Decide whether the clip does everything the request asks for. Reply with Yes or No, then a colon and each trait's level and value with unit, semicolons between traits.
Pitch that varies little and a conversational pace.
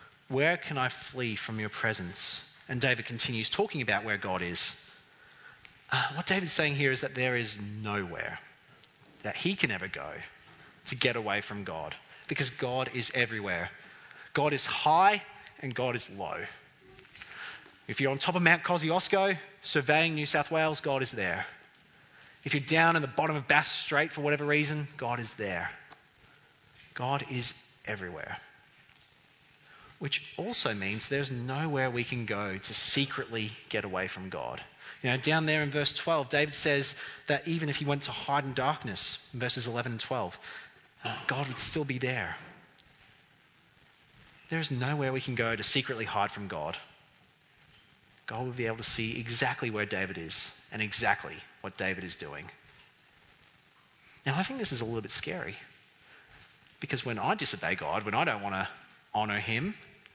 No: average, 4.7 semitones; average, 170 wpm